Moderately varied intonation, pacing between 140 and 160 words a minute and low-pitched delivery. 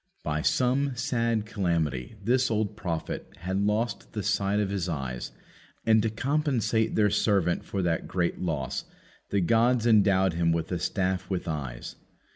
Yes: average, 4.8 semitones; average, 155 wpm; low, 100 Hz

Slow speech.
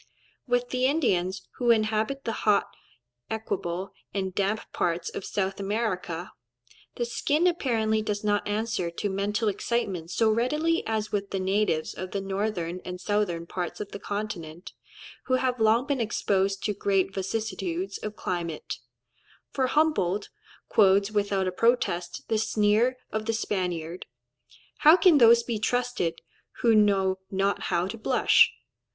No: average, 145 wpm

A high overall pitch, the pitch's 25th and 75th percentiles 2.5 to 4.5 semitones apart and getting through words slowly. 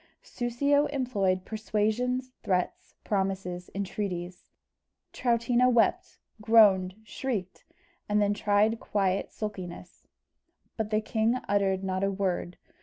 Yes: high, 205 Hz; average, 3.3 semitones; slow, 105 wpm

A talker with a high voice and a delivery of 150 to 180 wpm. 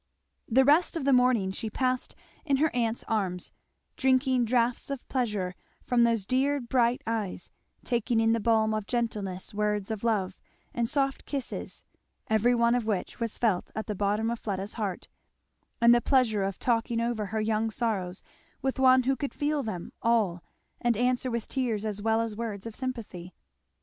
Yes: high, 230 Hz; average, 175 wpm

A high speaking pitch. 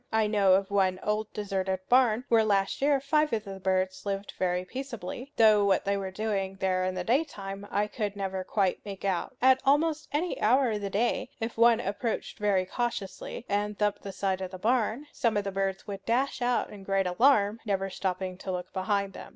Yes: high, 205 Hz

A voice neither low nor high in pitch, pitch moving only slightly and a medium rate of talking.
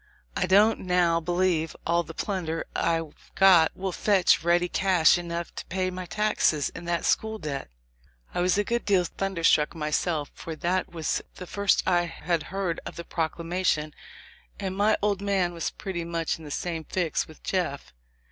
Yes: medium, 175 Hz; narrow, 2.3 semitones; average, 175 wpm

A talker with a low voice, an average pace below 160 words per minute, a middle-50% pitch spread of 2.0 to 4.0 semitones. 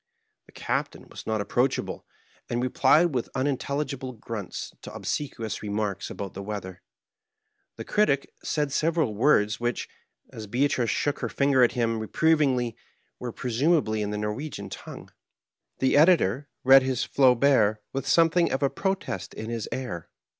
No: low, 125 Hz; average, 145 wpm; average, 4.6 semitones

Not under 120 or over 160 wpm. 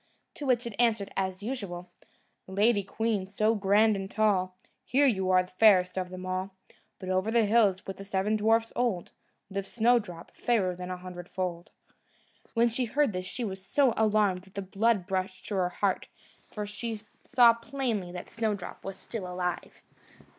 No: average, 170 wpm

